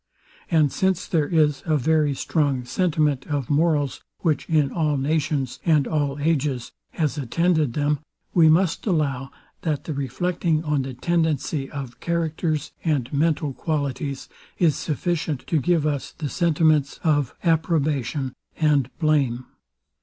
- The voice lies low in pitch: No, medium, 150 Hz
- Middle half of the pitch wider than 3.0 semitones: No, narrow, 2.5 semitones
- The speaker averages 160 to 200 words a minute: No, slow, 135 wpm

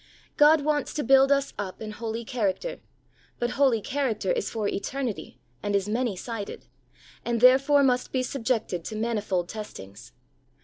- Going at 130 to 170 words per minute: Yes, average, 150 wpm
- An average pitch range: Yes, average, 4.5 semitones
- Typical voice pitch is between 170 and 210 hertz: No, high, 235 Hz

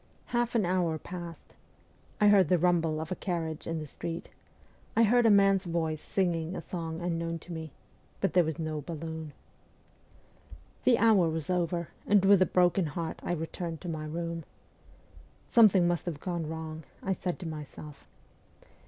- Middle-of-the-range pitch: Yes, medium, 170 Hz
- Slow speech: No, average, 170 wpm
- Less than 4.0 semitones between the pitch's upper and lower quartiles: Yes, narrow, 2.5 semitones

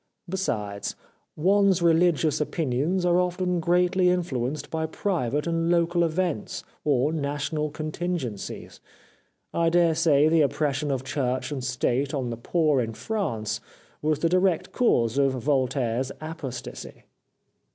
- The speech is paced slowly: Yes, slow, 125 wpm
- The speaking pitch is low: No, medium, 155 Hz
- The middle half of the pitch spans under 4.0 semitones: No, average, 4.6 semitones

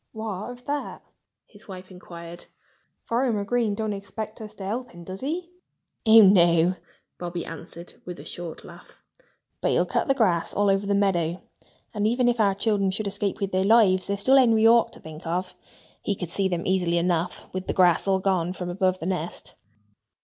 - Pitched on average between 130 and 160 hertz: No, high, 195 Hz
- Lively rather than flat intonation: No, average, 3.5 semitones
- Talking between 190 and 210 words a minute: Yes, average, 195 wpm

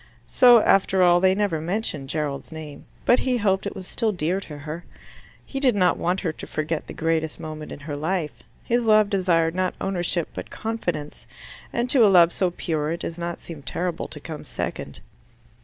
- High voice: No, medium, 175 Hz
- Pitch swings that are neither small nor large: Yes, average, 3.8 semitones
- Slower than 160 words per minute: No, average, 195 wpm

